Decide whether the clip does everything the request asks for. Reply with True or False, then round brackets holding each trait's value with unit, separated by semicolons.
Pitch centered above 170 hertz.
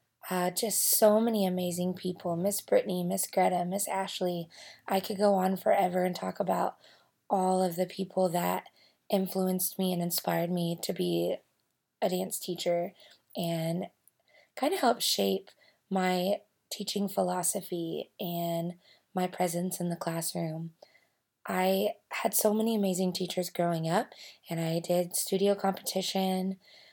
True (185 Hz)